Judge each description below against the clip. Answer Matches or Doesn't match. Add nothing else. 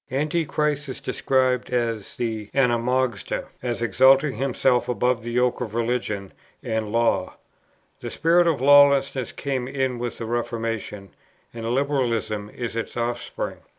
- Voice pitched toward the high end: Doesn't match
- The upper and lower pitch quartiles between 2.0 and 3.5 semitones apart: Matches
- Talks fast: Doesn't match